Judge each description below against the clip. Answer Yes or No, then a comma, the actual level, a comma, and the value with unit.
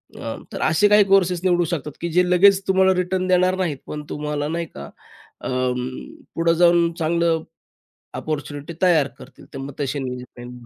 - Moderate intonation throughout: Yes, average, 3.7 semitones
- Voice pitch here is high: No, medium, 170 Hz